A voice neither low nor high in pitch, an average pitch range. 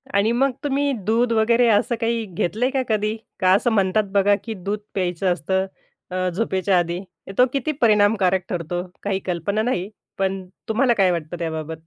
No: high, 200 Hz; average, 3.9 semitones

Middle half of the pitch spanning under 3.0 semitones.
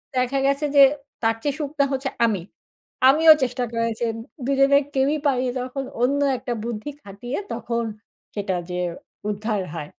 No: average, 3.7 semitones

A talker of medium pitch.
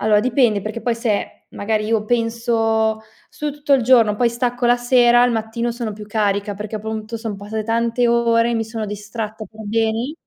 No: high, 225 Hz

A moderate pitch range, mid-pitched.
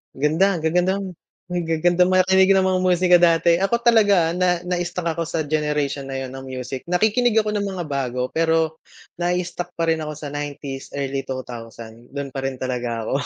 Yes: average, 4.9 semitones; medium, 165 Hz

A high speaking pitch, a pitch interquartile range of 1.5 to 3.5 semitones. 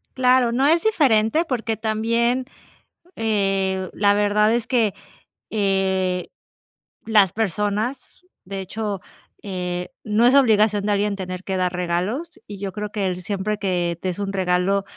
Yes: high, 205 Hz; average, 2.9 semitones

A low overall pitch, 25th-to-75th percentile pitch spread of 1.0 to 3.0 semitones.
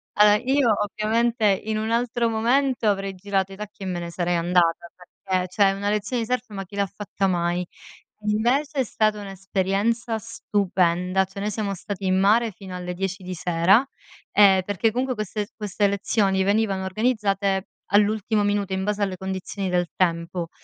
No: high, 200 Hz; narrow, 2.6 semitones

